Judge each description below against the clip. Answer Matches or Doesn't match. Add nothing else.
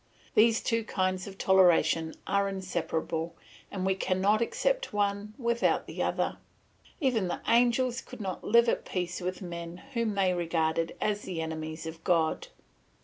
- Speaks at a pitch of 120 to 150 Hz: Doesn't match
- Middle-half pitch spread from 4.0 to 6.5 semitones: Matches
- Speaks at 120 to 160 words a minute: Matches